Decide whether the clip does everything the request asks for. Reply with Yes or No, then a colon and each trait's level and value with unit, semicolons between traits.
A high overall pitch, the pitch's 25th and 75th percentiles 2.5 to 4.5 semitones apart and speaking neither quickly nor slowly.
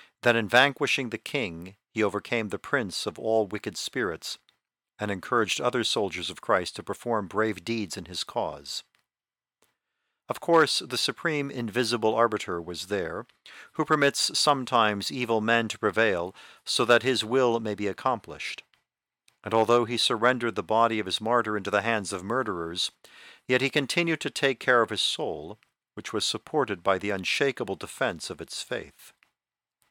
No: low, 115 Hz; average, 3.3 semitones; average, 165 wpm